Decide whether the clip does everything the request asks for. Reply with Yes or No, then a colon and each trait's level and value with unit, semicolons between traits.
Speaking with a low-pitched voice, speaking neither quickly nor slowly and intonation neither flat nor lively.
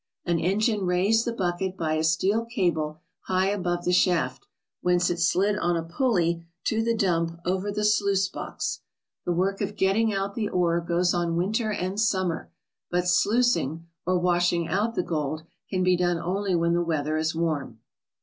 No: medium, 180 Hz; average, 180 wpm; average, 3.0 semitones